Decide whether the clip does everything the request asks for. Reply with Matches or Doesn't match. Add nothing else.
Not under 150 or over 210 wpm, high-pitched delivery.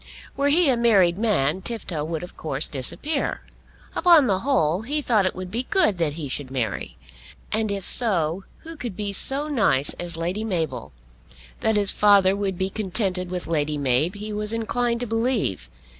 Matches